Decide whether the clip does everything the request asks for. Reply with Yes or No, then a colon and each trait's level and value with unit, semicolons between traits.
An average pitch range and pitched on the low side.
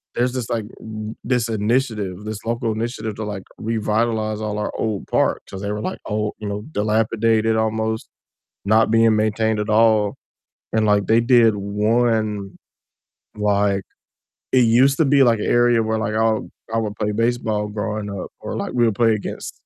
No: narrow, 1.5 semitones; low, 110 Hz